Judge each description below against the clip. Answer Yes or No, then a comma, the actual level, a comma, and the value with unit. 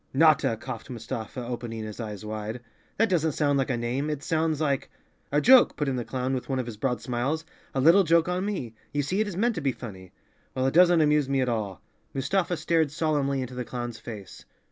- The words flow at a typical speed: No, fast, 225 wpm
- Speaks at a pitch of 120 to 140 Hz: Yes, low, 135 Hz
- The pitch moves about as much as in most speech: Yes, average, 5.0 semitones